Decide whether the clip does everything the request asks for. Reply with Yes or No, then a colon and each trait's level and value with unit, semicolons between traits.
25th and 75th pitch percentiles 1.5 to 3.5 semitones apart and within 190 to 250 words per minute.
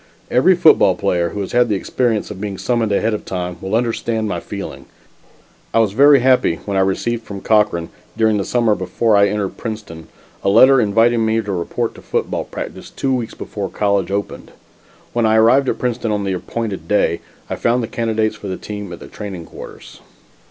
Yes: average, 3.0 semitones; average, 200 wpm